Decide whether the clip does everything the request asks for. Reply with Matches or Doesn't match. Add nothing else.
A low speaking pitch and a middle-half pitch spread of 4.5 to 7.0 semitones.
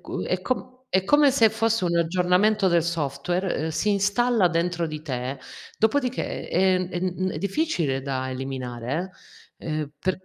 Doesn't match